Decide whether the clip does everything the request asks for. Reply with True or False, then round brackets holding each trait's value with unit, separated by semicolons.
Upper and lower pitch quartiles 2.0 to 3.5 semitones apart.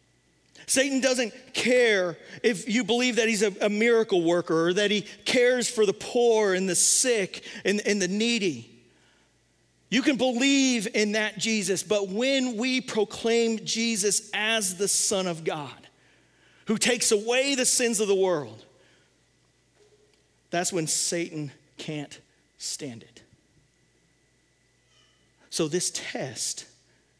False (4.6 semitones)